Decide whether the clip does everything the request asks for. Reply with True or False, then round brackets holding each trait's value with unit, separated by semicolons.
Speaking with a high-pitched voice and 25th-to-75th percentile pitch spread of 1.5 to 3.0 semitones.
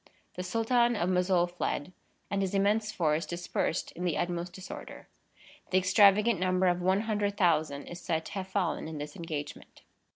False (180 Hz; 2.7 semitones)